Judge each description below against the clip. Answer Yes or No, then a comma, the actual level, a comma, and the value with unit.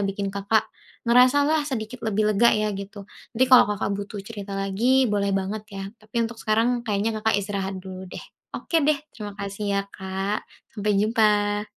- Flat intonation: Yes, narrow, 2.3 semitones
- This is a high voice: Yes, high, 210 Hz